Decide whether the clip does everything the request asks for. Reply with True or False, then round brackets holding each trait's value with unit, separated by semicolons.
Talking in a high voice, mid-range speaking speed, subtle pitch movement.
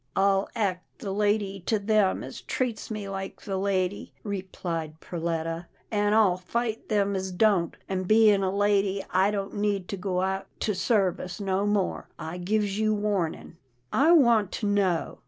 True (195 Hz; 175 wpm; 2.2 semitones)